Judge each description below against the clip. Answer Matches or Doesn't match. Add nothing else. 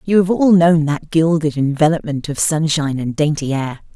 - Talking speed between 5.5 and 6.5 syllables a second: Doesn't match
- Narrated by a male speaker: Doesn't match